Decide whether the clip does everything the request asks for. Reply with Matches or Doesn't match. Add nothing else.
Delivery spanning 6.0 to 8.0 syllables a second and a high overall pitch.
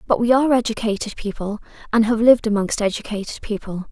Matches